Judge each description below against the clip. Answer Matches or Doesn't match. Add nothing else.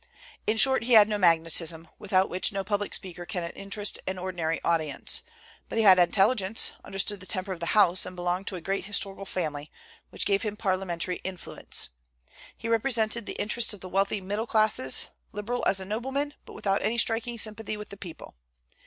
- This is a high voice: Matches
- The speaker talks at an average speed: Matches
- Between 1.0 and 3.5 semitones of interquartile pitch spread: Matches